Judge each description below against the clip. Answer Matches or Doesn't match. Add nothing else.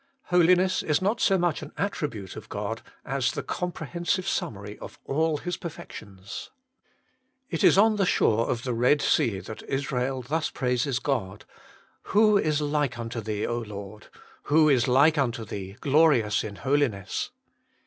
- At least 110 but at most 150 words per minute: Doesn't match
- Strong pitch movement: Matches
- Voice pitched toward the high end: Doesn't match